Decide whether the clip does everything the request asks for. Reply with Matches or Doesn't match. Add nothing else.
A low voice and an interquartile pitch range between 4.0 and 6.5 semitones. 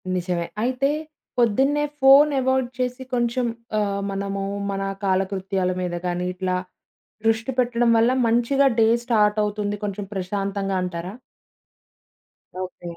Doesn't match